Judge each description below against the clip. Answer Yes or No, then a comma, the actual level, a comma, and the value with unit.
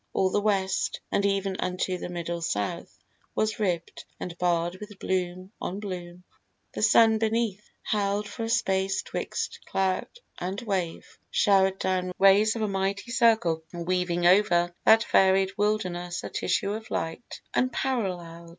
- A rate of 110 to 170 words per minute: Yes, average, 145 wpm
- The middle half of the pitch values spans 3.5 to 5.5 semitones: No, average, 2.9 semitones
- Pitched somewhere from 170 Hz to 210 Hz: Yes, high, 190 Hz